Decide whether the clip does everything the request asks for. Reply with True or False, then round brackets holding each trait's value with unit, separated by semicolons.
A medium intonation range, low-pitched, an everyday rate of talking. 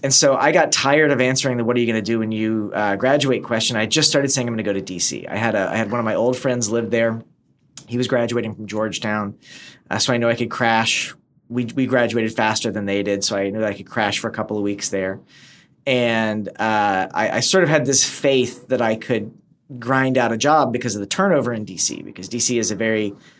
False (3.0 semitones; 115 Hz; 255 wpm)